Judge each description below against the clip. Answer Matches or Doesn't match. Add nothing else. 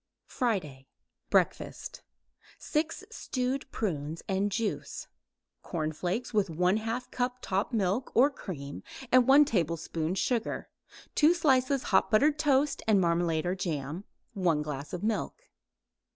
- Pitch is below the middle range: Doesn't match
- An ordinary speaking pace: Doesn't match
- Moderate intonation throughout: Doesn't match